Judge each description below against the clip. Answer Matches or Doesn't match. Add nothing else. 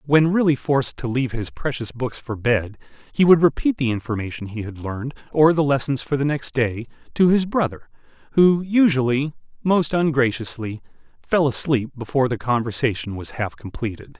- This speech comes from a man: Matches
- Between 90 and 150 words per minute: Doesn't match